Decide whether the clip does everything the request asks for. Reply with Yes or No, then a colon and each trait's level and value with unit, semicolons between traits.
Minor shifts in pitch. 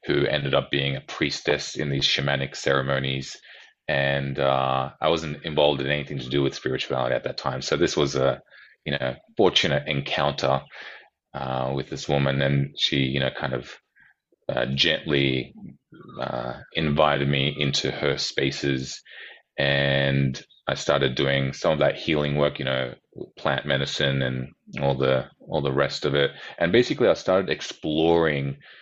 Yes: narrow, 1.1 semitones